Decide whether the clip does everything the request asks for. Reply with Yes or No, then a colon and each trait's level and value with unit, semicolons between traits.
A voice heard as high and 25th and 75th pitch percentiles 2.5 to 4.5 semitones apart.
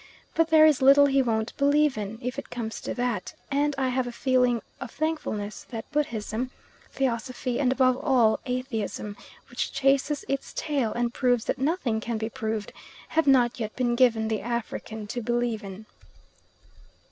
Yes: high, 245 Hz; average, 3.5 semitones